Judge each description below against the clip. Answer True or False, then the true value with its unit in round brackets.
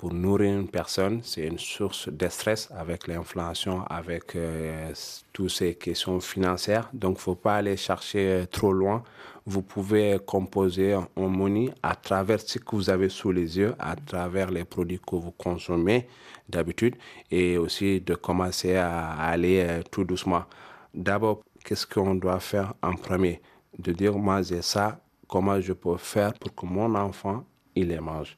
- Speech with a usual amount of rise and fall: False (2.3 semitones)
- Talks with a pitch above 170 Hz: False (95 Hz)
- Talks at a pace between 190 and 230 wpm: False (165 wpm)